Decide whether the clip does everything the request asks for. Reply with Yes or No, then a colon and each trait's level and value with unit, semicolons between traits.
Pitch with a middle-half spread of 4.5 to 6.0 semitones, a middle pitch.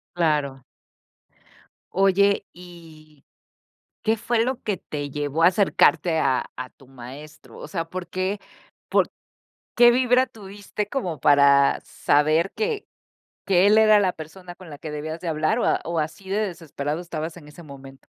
Yes: average, 5.0 semitones; medium, 170 Hz